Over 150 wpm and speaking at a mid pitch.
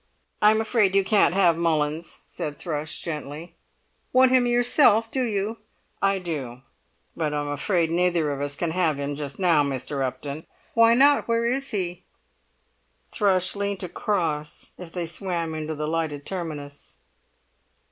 No: average, 145 wpm; medium, 170 Hz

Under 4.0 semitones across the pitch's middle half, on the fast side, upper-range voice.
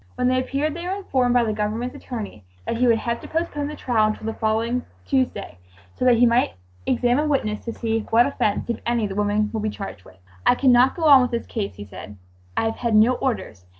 Yes: average, 3.1 semitones; fast, 235 wpm; high, 235 Hz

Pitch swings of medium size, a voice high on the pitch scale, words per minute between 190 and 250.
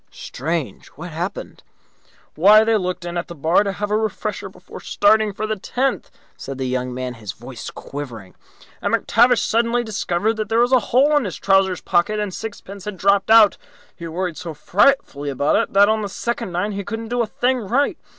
Yes: average, 4.7 semitones; high, 200 Hz; average, 200 wpm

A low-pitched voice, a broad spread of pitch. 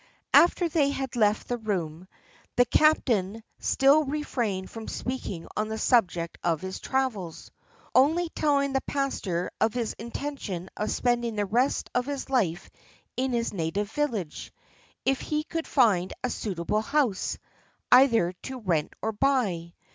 No: high, 235 Hz; wide, 6.1 semitones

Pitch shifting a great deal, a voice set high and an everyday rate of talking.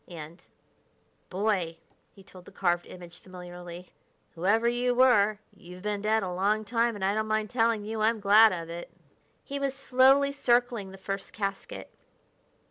No: average, 4.2 semitones; high, 205 Hz; average, 160 wpm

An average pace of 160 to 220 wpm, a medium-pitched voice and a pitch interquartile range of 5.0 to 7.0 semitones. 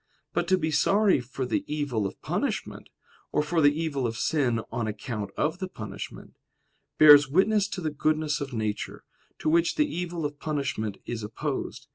Yes: average, 175 wpm; medium, 145 Hz; wide, 5.6 semitones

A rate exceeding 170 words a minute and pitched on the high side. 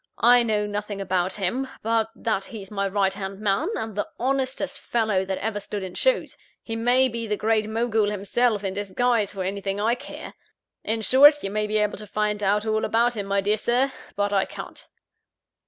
Yes: average, 200 wpm; high, 210 Hz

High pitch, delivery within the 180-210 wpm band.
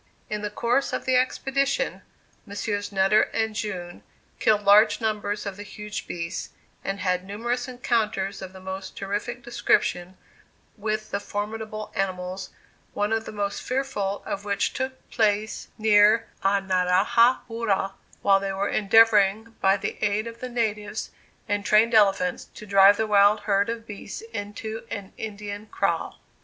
No: high, 210 Hz; average, 150 wpm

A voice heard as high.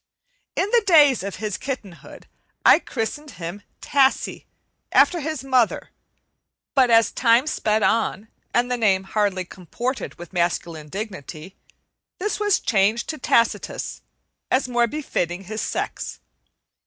Yes: high, 230 Hz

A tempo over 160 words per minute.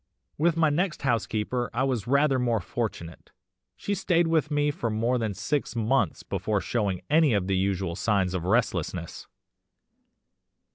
No: average, 150 wpm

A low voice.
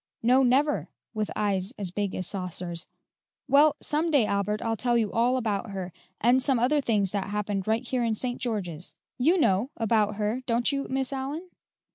No: high, 225 Hz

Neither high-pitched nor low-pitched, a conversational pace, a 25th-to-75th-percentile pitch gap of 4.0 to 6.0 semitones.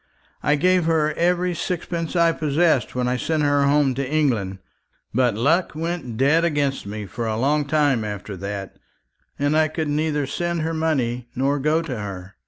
Yes: medium, 145 Hz; average, 180 wpm; average, 4.7 semitones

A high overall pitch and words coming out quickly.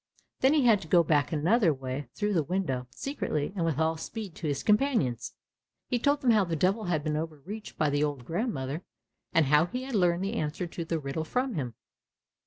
No: medium, 165 Hz; fast, 210 wpm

